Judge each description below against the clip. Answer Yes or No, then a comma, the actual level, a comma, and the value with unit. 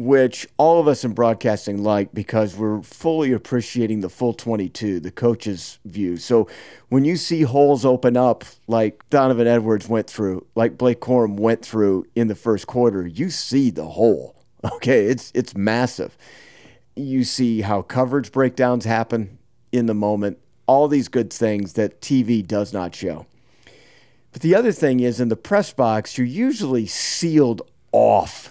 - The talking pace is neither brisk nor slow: Yes, average, 160 wpm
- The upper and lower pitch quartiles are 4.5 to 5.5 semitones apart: No, average, 3.4 semitones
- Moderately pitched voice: No, low, 120 Hz